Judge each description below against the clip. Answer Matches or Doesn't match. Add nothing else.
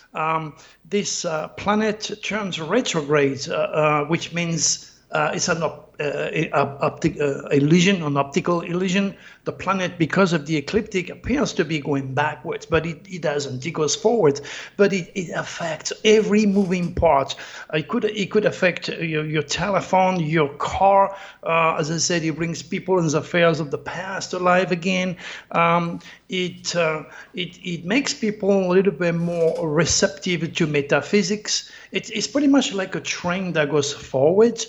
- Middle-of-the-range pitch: Matches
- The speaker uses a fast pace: Doesn't match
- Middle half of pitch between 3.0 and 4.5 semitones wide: Matches